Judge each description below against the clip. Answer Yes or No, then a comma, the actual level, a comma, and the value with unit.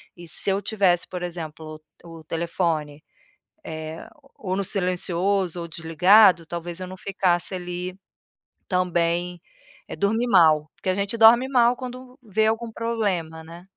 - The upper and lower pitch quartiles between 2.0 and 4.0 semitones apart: Yes, average, 3.3 semitones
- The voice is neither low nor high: Yes, medium, 180 Hz